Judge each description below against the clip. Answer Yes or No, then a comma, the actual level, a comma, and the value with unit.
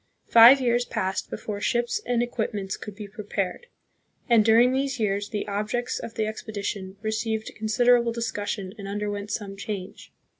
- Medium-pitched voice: No, high, 215 Hz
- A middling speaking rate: Yes, average, 155 wpm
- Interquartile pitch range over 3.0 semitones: No, average, 2.7 semitones